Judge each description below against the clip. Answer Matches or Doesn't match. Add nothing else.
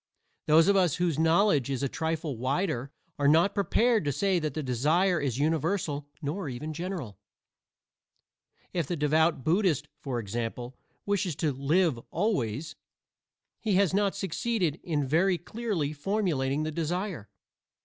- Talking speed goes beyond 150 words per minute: Doesn't match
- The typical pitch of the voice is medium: Matches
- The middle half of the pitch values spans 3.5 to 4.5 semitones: Doesn't match